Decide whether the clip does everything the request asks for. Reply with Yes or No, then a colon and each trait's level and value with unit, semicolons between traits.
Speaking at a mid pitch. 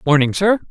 Yes: medium, 170 Hz